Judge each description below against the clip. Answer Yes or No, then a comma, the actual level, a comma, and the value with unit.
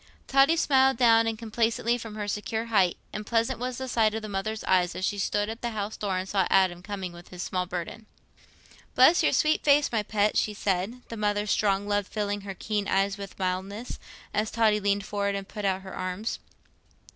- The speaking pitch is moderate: No, high, 210 Hz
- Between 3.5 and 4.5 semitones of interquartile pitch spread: No, average, 2.7 semitones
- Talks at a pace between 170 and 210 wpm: Yes, fast, 205 wpm